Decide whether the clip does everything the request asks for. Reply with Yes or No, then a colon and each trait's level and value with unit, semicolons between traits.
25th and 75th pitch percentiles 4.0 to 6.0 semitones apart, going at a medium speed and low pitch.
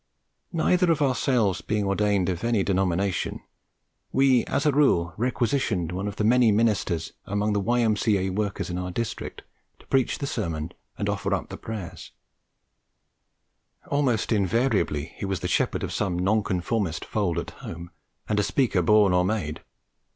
Yes: average, 4.4 semitones; average, 155 wpm; low, 105 Hz